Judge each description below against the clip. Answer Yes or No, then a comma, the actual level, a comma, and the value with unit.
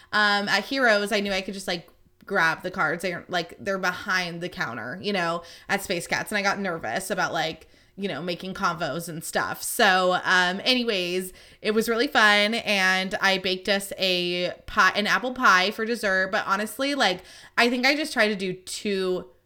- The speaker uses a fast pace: No, average, 195 wpm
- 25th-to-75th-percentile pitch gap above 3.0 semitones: No, average, 2.7 semitones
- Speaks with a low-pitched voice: No, high, 195 Hz